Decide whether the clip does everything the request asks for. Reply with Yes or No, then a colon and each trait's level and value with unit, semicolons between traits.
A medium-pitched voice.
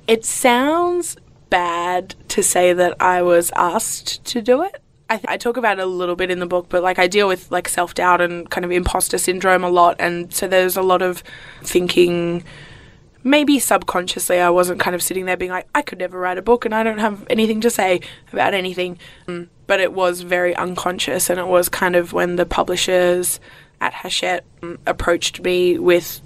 Yes: medium, 180 Hz